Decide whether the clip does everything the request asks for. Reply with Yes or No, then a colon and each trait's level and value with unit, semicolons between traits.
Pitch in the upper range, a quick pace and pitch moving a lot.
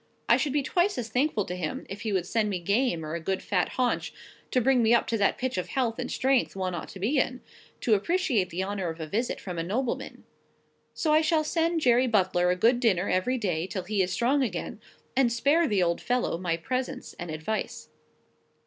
Yes: high, 220 Hz; fast, 230 wpm; wide, 6.0 semitones